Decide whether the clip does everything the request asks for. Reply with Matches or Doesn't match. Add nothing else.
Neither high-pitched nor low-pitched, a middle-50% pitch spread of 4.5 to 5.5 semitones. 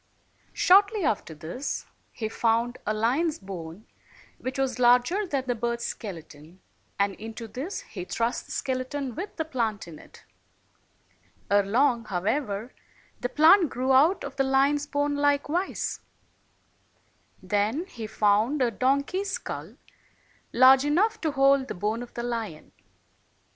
Doesn't match